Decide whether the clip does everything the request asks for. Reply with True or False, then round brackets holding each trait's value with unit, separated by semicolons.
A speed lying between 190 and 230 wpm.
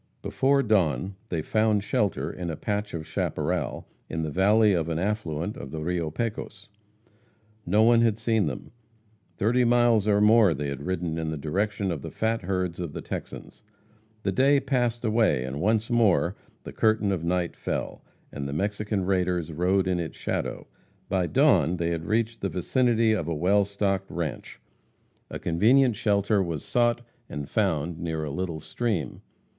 False (170 wpm)